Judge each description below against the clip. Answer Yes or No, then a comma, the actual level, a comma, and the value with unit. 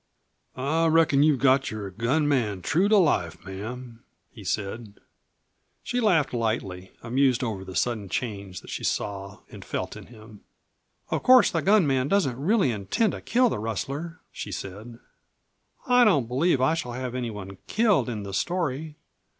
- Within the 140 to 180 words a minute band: Yes, average, 165 wpm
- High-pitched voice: No, low, 125 Hz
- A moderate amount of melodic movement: No, wide, 7.4 semitones